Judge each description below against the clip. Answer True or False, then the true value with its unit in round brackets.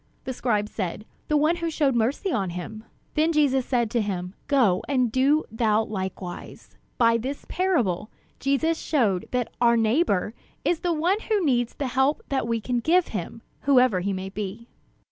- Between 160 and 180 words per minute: True (175 wpm)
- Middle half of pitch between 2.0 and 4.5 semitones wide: False (5.6 semitones)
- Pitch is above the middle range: True (245 Hz)